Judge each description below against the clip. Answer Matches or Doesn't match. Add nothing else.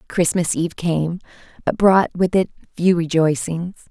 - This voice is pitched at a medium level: Matches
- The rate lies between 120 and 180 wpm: Matches